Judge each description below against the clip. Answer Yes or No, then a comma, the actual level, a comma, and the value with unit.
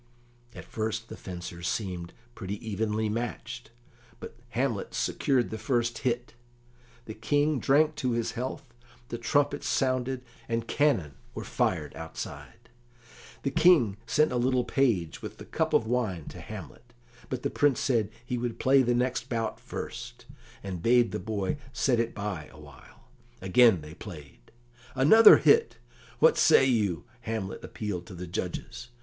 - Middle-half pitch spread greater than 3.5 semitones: Yes, average, 4.2 semitones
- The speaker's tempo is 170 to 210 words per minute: No, average, 150 wpm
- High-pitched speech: No, low, 115 Hz